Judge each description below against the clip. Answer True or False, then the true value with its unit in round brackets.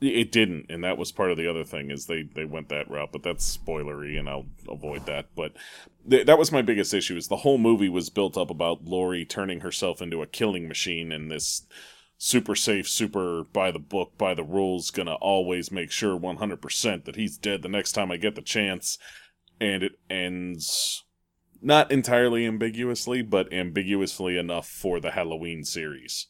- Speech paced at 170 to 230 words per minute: True (190 wpm)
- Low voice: True (90 Hz)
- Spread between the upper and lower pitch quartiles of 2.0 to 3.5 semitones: False (4.2 semitones)